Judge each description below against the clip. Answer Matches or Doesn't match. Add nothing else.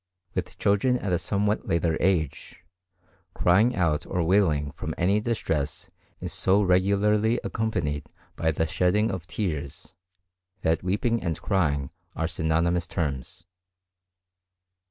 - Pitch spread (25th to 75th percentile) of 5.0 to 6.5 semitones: Doesn't match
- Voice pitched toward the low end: Matches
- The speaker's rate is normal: Doesn't match